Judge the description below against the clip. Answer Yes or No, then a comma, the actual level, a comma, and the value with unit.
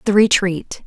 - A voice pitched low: No, high, 195 Hz